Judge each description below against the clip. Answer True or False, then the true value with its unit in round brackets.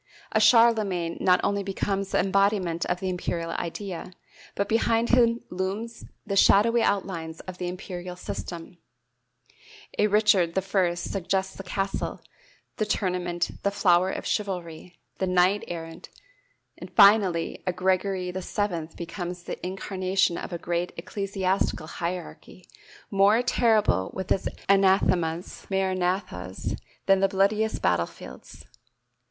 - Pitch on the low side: False (190 Hz)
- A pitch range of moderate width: False (2.2 semitones)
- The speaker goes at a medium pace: False (120 wpm)